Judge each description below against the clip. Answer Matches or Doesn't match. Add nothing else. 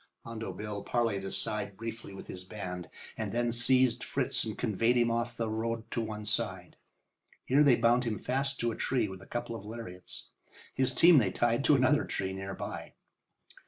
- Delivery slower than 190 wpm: Doesn't match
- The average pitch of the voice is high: Doesn't match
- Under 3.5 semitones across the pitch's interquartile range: Matches